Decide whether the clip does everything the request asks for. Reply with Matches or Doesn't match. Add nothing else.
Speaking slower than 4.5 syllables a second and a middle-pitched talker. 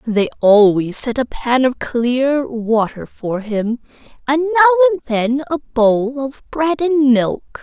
Doesn't match